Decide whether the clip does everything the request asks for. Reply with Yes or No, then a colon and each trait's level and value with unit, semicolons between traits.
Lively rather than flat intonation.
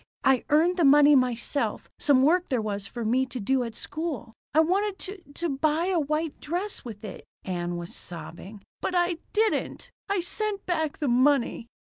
Yes: wide, 6.4 semitones